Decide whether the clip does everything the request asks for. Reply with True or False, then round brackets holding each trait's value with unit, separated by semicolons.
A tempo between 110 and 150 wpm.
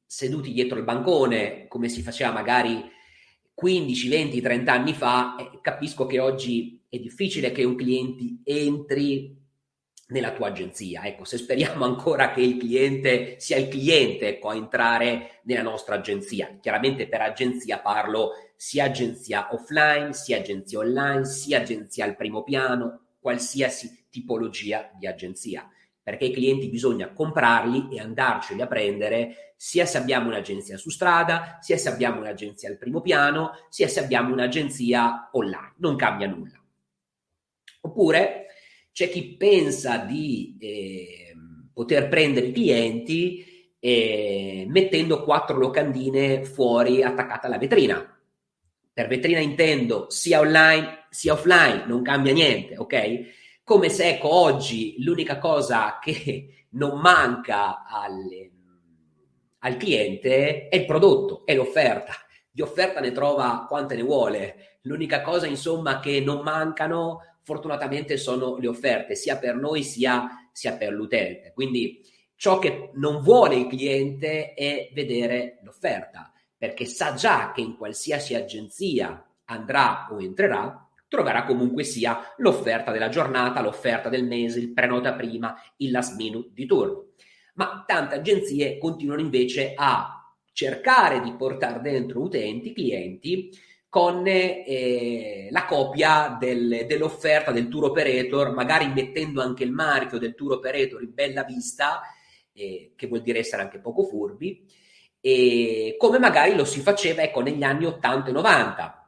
True (140 wpm)